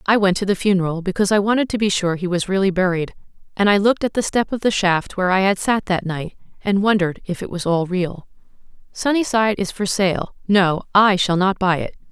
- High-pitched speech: Yes, high, 195 Hz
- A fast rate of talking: Yes, fast, 230 wpm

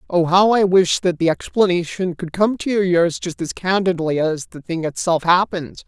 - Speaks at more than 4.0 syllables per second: Yes, 5.0 syllables/s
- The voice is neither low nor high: Yes, medium, 180 Hz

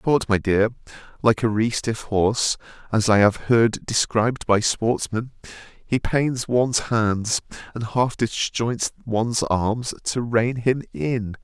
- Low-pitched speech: Yes, low, 115 Hz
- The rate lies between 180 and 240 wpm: No, average, 145 wpm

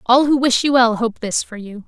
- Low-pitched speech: No, high, 240 Hz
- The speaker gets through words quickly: Yes, fast, 290 wpm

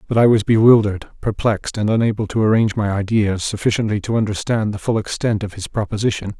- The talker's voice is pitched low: Yes, low, 105 Hz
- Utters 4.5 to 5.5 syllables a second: No, 6.5 syllables/s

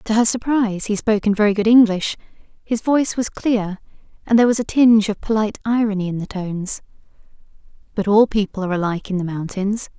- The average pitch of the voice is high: Yes, high, 210 Hz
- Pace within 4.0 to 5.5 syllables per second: No, 6.2 syllables/s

